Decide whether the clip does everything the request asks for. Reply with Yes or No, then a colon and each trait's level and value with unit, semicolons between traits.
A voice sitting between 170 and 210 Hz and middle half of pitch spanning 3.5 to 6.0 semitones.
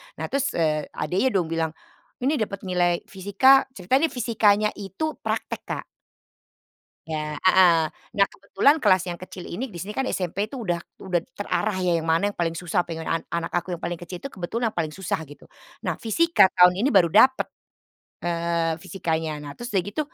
Yes: medium, 185 Hz; average, 3.8 semitones